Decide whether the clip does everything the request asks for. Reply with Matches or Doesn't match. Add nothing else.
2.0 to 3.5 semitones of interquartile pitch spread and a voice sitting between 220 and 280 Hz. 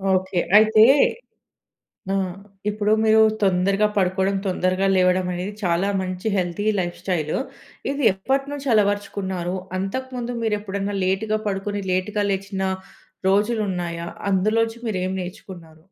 Doesn't match